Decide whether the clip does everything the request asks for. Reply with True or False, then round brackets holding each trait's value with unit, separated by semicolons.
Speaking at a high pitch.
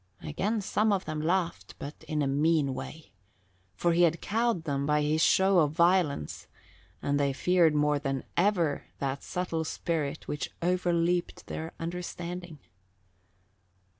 False (165 Hz)